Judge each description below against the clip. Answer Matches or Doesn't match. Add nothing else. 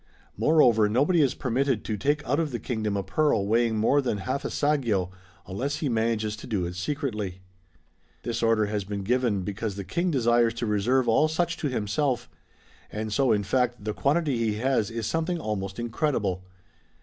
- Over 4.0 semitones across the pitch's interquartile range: Matches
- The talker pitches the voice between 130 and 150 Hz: Doesn't match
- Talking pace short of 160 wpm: Doesn't match